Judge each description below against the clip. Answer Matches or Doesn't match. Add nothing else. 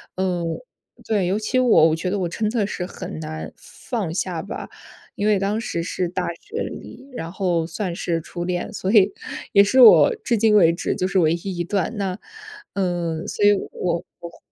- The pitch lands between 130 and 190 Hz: Matches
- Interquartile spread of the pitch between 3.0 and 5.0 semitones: Matches